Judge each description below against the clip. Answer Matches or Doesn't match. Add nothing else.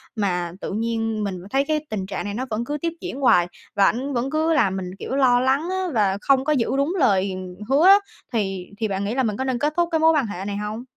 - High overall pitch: Matches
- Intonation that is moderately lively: Doesn't match